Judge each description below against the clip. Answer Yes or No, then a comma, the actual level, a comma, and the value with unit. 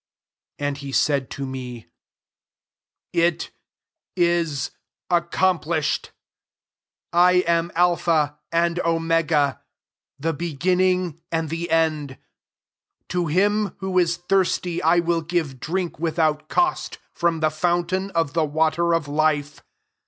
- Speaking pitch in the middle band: Yes, medium, 165 Hz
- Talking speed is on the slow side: Yes, slow, 115 wpm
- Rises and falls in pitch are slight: Yes, narrow, 2.3 semitones